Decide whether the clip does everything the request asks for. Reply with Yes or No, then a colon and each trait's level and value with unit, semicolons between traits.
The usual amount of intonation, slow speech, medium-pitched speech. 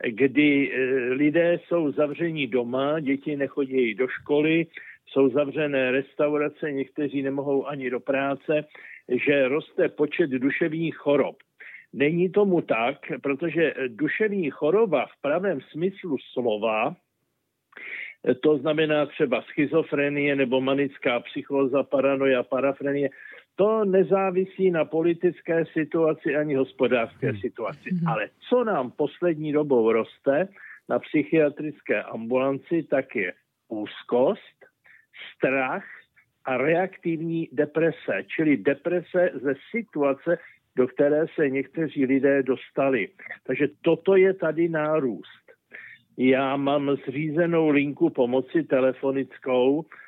Yes: average, 3.3 semitones; slow, 105 wpm; medium, 150 Hz